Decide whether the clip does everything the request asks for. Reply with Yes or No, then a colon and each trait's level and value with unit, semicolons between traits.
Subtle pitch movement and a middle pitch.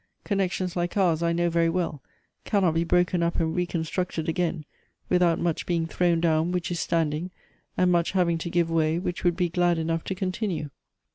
Yes: narrow, 1.5 semitones; medium, 170 Hz